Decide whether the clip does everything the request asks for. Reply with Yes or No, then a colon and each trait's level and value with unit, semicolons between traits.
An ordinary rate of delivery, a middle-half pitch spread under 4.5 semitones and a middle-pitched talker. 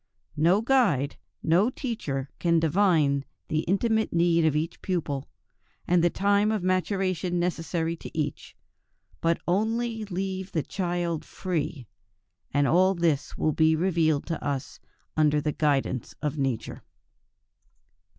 No: slow, 130 wpm; average, 3.9 semitones; medium, 170 Hz